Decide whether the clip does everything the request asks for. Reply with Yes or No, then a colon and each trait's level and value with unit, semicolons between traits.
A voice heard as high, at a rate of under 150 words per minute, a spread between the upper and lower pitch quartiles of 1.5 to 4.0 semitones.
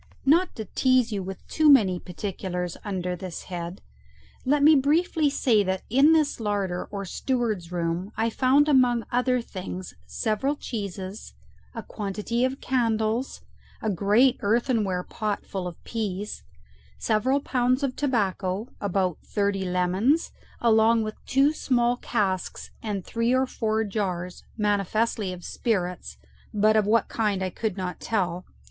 No: high, 215 Hz; average, 140 wpm; average, 4.8 semitones